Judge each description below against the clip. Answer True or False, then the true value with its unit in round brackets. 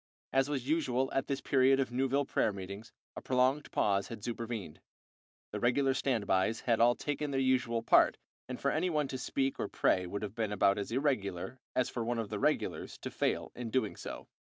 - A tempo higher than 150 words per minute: True (205 wpm)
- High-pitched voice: False (125 Hz)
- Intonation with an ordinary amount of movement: True (3.6 semitones)